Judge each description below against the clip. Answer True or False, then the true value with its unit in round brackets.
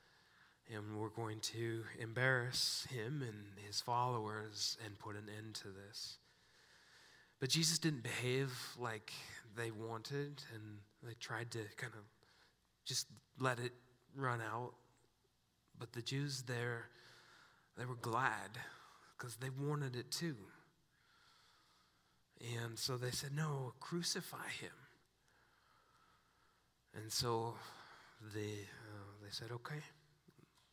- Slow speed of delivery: True (115 wpm)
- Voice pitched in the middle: False (120 Hz)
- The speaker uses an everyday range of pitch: True (3.2 semitones)